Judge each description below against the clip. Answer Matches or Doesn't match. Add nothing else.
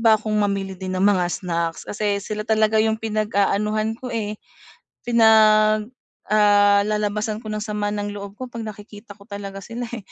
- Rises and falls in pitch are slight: Matches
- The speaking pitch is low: Doesn't match